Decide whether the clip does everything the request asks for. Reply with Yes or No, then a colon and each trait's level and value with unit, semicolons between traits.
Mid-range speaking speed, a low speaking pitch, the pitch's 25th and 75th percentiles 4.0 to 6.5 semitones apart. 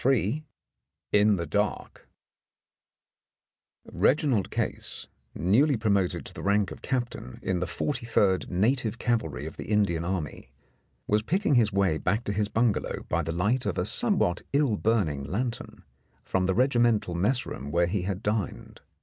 Yes: average, 155 wpm; low, 105 Hz; average, 4.5 semitones